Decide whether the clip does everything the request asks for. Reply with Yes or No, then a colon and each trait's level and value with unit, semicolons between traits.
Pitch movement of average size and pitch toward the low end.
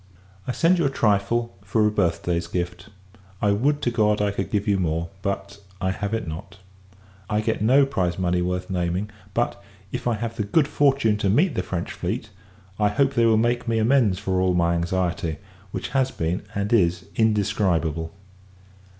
Yes: average, 4.2 semitones; low, 100 Hz